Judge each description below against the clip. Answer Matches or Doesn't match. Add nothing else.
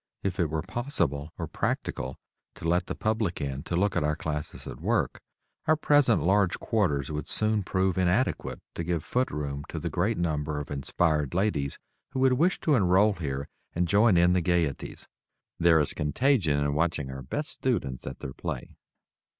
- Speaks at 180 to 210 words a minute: Matches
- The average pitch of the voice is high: Doesn't match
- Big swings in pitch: Matches